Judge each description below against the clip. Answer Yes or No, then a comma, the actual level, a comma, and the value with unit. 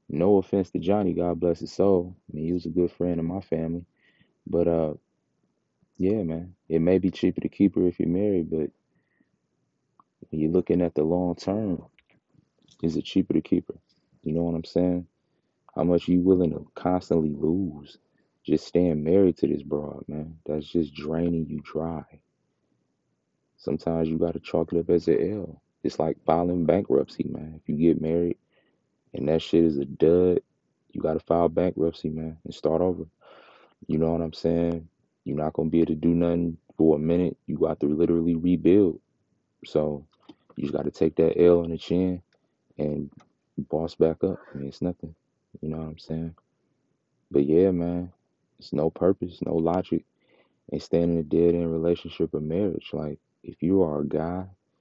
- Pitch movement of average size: No, narrow, 1.9 semitones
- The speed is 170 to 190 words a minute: Yes, average, 185 wpm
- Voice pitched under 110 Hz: Yes, very low, 85 Hz